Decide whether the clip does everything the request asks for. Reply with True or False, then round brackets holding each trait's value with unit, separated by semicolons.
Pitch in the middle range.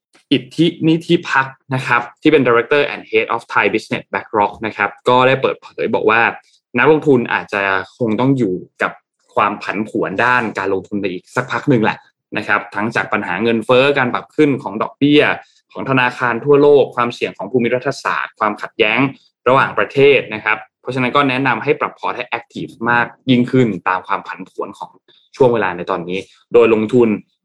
False (120 Hz)